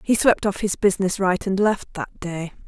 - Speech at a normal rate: No, fast, 225 wpm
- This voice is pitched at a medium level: No, high, 195 Hz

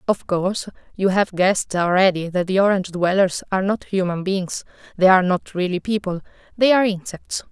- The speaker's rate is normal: Yes, average, 175 wpm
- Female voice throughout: Yes, female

